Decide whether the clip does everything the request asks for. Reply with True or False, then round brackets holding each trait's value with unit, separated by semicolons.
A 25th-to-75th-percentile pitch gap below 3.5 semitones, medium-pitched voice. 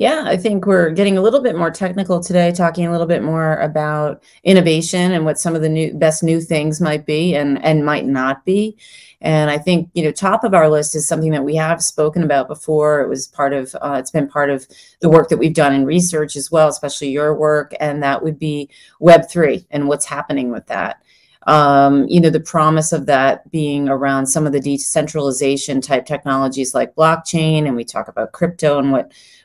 True (2.5 semitones; 155 Hz)